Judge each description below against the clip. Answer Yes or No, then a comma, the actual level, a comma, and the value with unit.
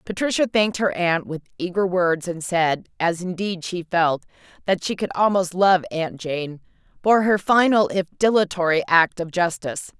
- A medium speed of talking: Yes, average, 170 wpm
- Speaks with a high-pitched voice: No, medium, 180 Hz